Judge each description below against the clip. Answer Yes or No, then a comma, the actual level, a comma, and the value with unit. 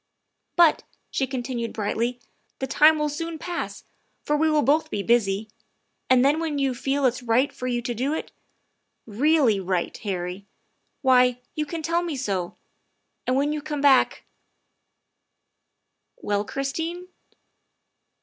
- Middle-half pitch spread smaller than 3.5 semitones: No, average, 4.4 semitones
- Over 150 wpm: Yes, average, 160 wpm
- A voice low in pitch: No, very high, 265 Hz